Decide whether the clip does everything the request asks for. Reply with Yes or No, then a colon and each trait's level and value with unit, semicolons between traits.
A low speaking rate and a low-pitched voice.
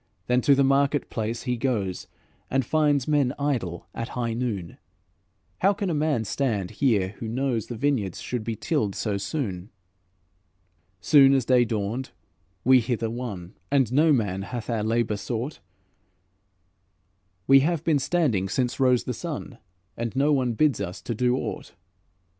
No: average, 160 wpm; low, 125 Hz